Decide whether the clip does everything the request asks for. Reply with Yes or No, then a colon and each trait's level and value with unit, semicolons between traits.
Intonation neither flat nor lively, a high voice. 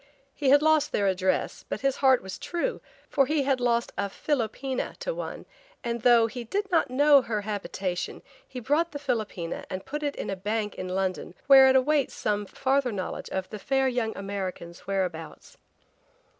No: wide, 5.9 semitones; high, 240 Hz